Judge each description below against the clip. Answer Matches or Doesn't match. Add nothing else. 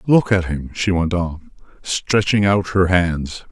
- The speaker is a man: Matches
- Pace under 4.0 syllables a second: Matches